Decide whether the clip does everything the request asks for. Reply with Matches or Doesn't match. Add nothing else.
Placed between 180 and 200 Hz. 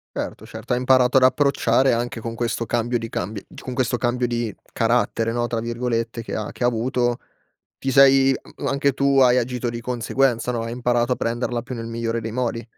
Doesn't match